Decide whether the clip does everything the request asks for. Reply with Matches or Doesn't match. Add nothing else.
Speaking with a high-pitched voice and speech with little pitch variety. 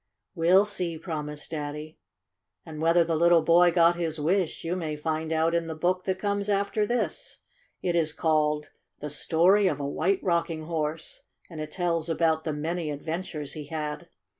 Doesn't match